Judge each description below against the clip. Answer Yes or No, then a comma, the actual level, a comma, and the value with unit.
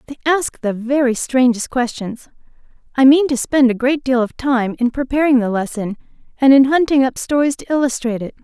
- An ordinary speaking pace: Yes, average, 190 wpm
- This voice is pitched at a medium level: No, very high, 260 Hz